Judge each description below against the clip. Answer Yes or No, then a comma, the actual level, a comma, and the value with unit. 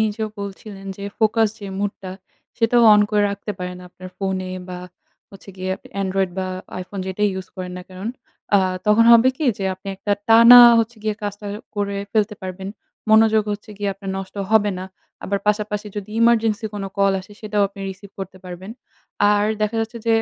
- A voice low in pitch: No, high, 205 Hz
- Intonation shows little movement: Yes, narrow, 2.3 semitones